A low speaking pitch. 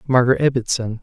Yes: low, 125 Hz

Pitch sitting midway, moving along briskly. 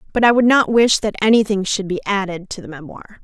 No: high, 205 Hz; fast, 240 wpm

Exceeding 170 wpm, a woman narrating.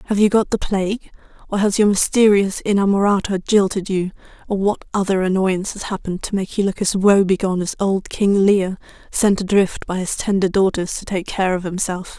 Yes: average, 190 wpm; female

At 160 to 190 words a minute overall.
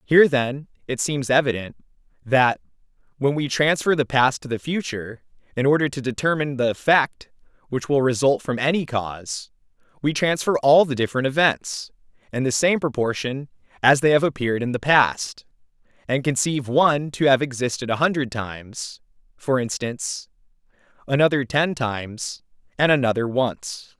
No: average, 150 wpm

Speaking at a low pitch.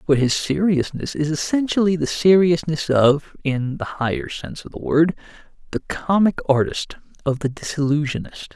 No: medium, 160 Hz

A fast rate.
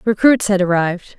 No: average, 150 wpm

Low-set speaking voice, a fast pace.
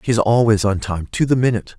Yes: low, 110 Hz; fast, 235 wpm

